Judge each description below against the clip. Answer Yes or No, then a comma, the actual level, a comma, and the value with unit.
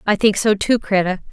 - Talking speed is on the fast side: Yes, fast, 225 wpm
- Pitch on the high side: Yes, high, 205 Hz